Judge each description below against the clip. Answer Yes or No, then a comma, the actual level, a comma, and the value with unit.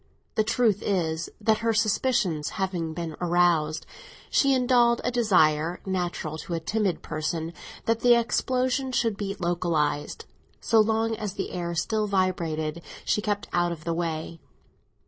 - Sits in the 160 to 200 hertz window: Yes, medium, 185 Hz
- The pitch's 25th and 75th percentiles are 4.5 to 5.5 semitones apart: Yes, average, 5.2 semitones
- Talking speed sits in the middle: Yes, average, 145 wpm